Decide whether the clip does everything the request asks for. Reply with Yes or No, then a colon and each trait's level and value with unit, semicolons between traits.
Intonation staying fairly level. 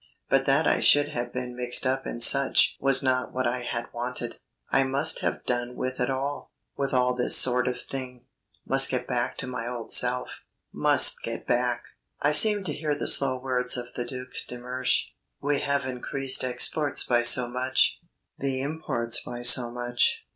Yes: narrow, 1.7 semitones